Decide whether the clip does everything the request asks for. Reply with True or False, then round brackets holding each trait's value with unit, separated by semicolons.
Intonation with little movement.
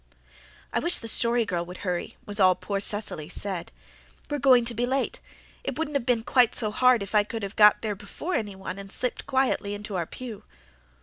False (3.9 semitones)